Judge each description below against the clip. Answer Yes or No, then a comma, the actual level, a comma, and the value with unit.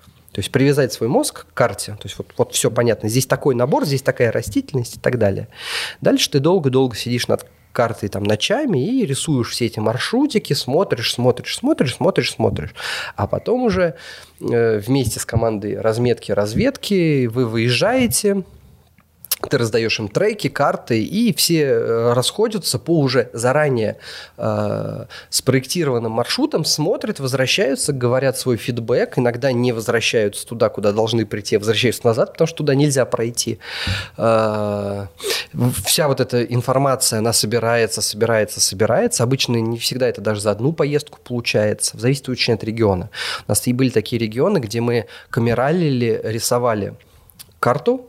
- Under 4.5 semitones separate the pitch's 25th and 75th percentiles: Yes, average, 4.0 semitones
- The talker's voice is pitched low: Yes, low, 125 Hz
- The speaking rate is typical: Yes, average, 145 wpm